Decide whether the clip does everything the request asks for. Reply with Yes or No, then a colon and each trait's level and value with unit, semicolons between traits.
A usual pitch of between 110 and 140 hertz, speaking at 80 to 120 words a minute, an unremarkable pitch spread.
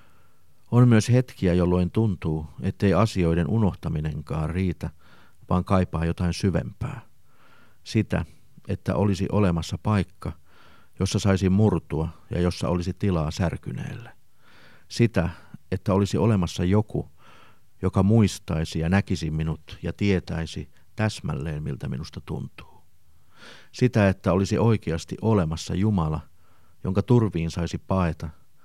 No: very low, 95 Hz; average, 110 wpm; average, 3.5 semitones